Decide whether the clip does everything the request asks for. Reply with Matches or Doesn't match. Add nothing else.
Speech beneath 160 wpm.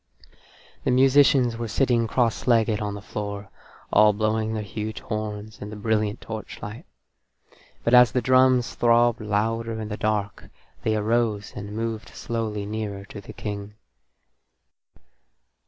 Matches